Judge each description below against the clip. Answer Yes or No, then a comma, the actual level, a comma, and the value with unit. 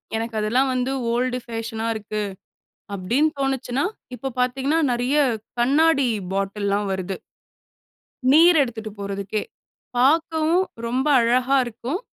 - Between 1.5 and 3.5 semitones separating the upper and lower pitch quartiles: No, average, 3.9 semitones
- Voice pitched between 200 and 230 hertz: No, high, 245 Hz